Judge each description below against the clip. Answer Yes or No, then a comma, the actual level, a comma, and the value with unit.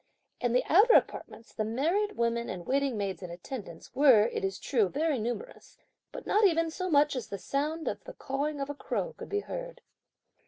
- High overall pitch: Yes, very high, 275 Hz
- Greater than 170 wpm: Yes, average, 200 wpm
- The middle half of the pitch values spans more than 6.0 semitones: Yes, wide, 6.5 semitones